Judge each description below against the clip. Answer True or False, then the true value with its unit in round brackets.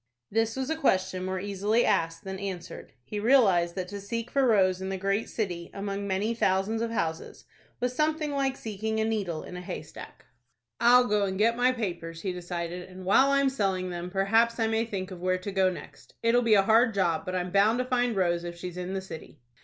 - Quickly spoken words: True (225 wpm)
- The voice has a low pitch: False (195 Hz)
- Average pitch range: True (3.9 semitones)